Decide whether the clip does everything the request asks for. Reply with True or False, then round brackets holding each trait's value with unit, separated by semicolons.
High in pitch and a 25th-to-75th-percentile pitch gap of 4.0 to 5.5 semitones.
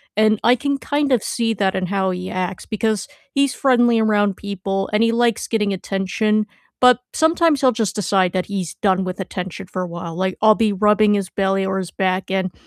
False (200 Hz; 3.2 semitones)